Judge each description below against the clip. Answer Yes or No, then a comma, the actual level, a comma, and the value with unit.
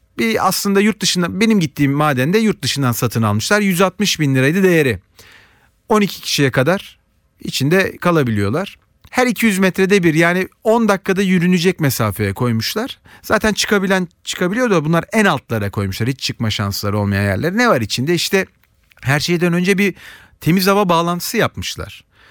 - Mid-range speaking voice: Yes, medium, 170 Hz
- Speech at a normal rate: No, fast, 150 wpm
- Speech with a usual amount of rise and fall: No, wide, 7.5 semitones